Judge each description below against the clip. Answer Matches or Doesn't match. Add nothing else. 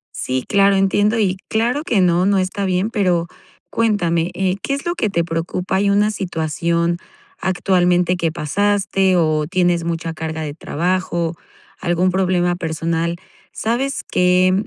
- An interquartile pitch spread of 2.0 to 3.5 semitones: Matches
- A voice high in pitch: Doesn't match